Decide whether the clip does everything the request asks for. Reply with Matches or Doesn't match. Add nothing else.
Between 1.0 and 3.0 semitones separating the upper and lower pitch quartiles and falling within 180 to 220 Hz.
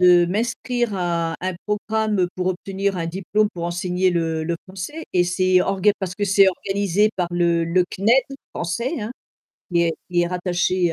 Matches